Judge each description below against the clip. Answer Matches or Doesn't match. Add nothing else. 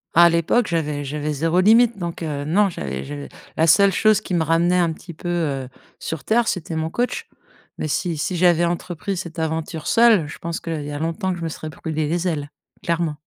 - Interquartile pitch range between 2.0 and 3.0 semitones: Matches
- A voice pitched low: Doesn't match